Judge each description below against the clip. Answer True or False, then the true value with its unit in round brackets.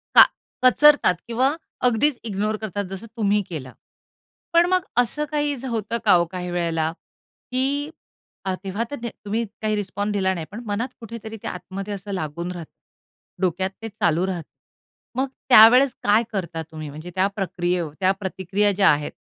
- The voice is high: True (200 Hz)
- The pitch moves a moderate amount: True (4.0 semitones)